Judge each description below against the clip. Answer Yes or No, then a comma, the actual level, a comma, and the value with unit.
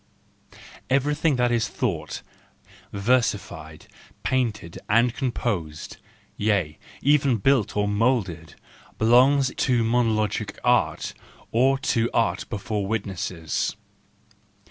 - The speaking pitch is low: Yes, low, 115 Hz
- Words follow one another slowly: Yes, slow, 100 wpm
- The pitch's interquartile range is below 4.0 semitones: No, average, 4.3 semitones